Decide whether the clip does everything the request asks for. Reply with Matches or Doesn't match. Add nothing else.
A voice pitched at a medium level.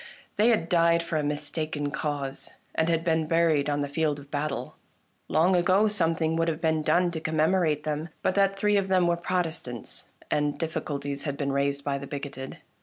Matches